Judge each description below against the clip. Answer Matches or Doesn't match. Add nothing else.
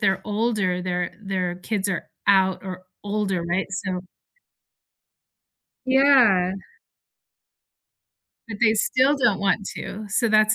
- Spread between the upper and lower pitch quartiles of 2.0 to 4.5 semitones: Matches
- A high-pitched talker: Matches